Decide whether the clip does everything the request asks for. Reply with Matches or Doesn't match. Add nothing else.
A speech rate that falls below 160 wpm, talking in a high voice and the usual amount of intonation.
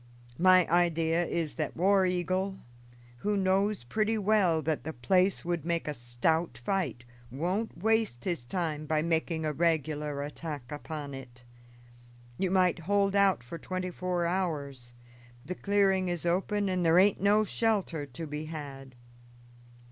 Doesn't match